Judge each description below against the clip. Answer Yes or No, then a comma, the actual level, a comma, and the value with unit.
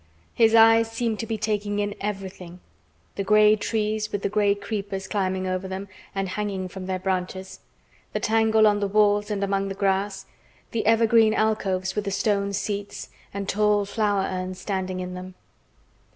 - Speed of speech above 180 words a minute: No, average, 165 wpm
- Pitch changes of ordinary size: No, narrow, 2.0 semitones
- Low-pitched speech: No, high, 200 Hz